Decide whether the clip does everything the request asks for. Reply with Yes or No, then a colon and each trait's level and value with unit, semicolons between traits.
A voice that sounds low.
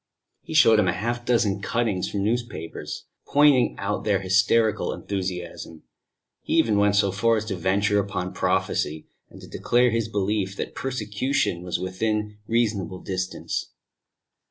Yes: low, 100 Hz